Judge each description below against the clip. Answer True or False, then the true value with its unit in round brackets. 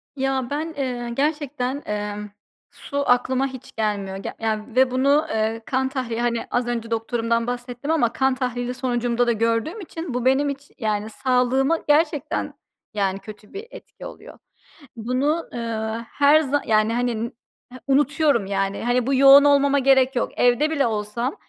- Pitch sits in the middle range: False (250 Hz)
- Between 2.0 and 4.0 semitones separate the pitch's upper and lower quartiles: True (3.4 semitones)